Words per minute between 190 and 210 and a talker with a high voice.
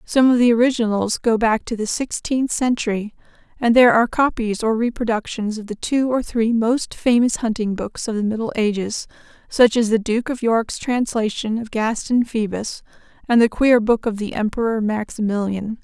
No: average, 180 wpm; high, 225 Hz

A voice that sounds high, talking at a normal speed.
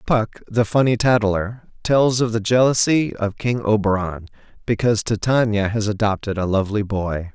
No: low, 110 Hz; average, 145 wpm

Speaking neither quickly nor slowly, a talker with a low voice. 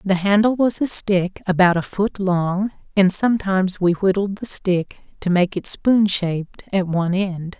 No: average, 180 wpm; high, 190 Hz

